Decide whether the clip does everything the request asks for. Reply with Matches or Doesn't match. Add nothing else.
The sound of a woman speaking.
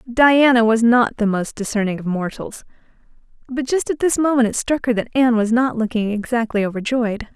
Matches